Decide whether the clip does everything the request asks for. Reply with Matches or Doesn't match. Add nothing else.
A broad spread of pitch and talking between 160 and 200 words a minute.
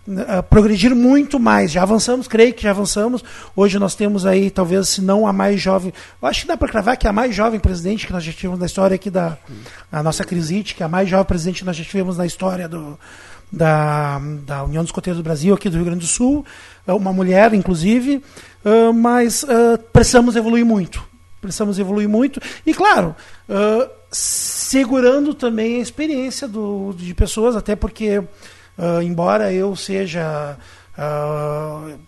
Doesn't match